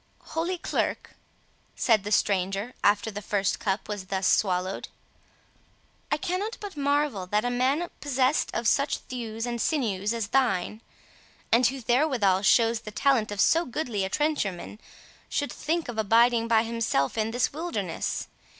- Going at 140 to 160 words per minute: Yes, average, 155 wpm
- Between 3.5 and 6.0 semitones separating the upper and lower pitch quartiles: Yes, average, 5.0 semitones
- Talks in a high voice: Yes, high, 230 Hz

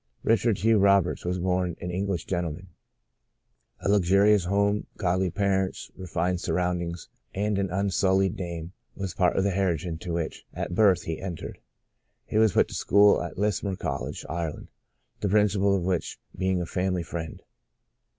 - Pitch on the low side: Yes, very low, 95 Hz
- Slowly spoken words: No, average, 160 wpm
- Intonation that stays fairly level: Yes, narrow, 2.2 semitones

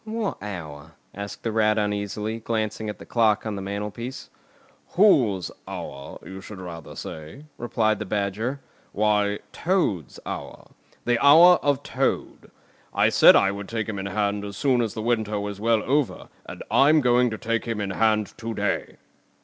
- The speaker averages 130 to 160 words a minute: No, average, 170 wpm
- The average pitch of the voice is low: Yes, low, 110 Hz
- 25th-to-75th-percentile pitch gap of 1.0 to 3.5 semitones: Yes, average, 2.9 semitones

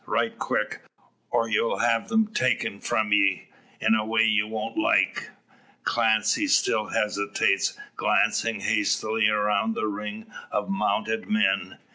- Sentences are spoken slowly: Yes, slow, 130 wpm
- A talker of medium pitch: No, low, 110 Hz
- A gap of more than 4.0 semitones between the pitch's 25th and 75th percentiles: No, average, 2.7 semitones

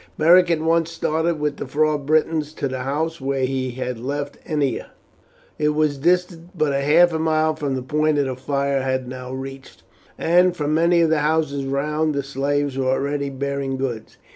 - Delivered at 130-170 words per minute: No, average, 185 wpm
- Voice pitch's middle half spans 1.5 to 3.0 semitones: Yes, average, 2.7 semitones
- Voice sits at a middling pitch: Yes, medium, 145 Hz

